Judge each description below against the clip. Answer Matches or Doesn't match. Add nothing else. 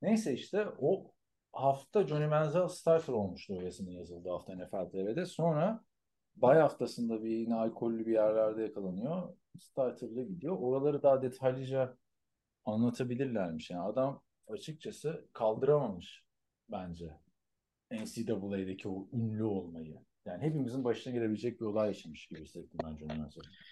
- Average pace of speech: Matches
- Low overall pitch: Matches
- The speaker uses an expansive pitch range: Matches